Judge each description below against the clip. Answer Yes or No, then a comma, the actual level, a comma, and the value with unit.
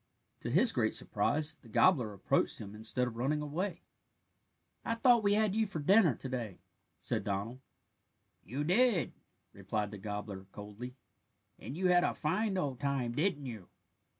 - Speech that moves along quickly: No, average, 160 wpm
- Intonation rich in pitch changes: Yes, wide, 8.8 semitones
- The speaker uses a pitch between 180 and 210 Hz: No, medium, 140 Hz